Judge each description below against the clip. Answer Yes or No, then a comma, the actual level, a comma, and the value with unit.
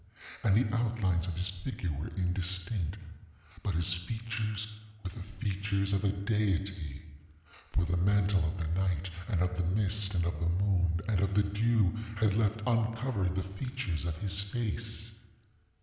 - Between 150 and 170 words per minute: Yes, average, 160 wpm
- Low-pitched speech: Yes, low, 100 Hz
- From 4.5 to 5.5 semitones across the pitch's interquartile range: No, average, 3.1 semitones